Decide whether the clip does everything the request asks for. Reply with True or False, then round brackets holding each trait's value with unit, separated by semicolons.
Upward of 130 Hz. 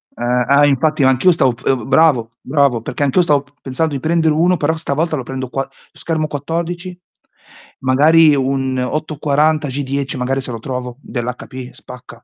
True (140 Hz)